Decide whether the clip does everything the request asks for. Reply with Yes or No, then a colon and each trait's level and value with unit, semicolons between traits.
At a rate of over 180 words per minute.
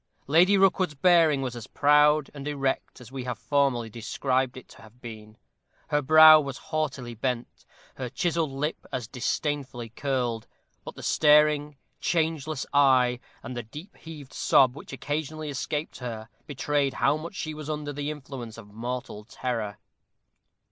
No: average, 155 wpm